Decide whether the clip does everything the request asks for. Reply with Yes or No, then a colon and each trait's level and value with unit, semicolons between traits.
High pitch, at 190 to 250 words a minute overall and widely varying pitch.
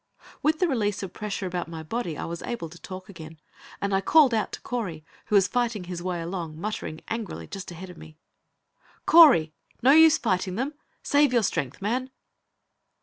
Yes: high, 195 Hz; average, 195 wpm; wide, 6.0 semitones